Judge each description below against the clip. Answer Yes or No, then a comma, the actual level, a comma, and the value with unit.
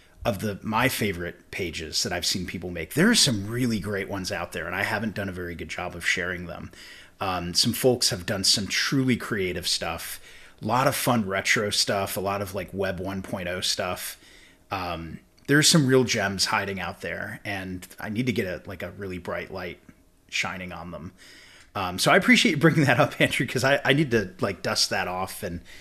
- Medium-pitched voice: No, low, 100 Hz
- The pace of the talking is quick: Yes, fast, 215 wpm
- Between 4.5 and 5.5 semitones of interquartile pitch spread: Yes, average, 5.1 semitones